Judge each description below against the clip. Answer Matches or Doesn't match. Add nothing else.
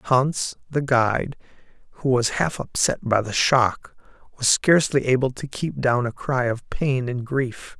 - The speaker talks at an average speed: Matches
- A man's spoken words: Matches